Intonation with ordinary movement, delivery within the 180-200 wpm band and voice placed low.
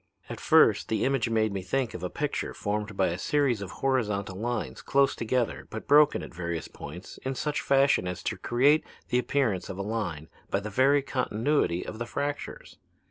No: wide, 5.7 semitones; average, 190 wpm; low, 115 Hz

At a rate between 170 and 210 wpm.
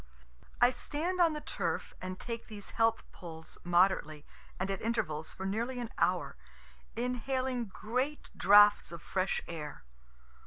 No: average, 140 wpm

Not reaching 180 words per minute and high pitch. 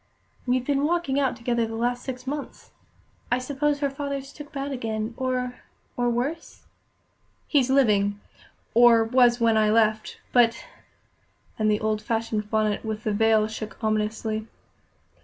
Yes: average, 150 wpm; high, 235 Hz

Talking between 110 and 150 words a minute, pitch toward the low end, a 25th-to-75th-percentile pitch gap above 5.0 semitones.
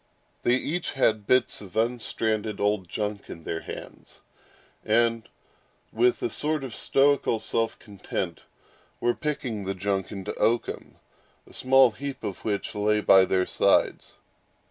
No: average, 140 wpm; low, 110 Hz; average, 3.5 semitones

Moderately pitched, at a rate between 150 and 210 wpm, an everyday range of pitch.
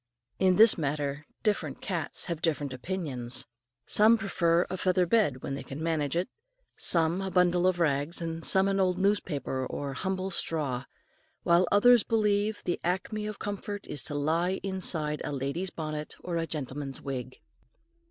Yes: medium, 170 Hz; average, 160 wpm; average, 4.7 semitones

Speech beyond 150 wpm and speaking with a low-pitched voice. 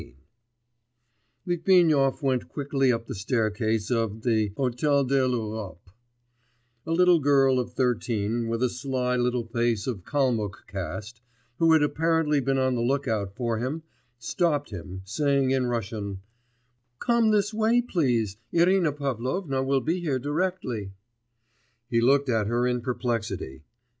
No: average, 140 wpm; low, 125 Hz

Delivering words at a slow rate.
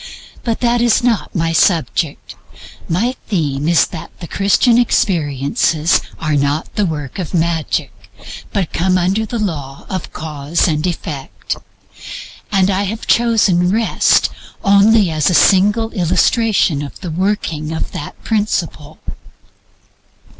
Yes: slow, 125 wpm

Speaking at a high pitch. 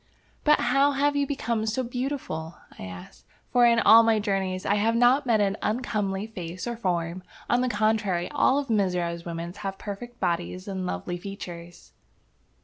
Yes: high, 205 Hz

